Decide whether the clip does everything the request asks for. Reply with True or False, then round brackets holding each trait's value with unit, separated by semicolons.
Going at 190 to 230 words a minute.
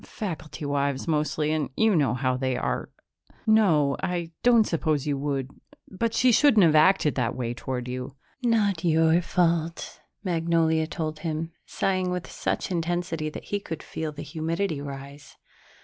False (155 wpm)